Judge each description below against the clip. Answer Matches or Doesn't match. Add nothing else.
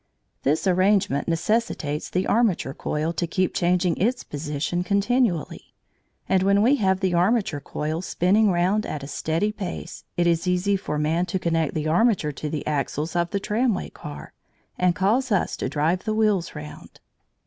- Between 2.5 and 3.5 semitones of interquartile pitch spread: Doesn't match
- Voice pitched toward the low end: Doesn't match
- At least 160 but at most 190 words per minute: Matches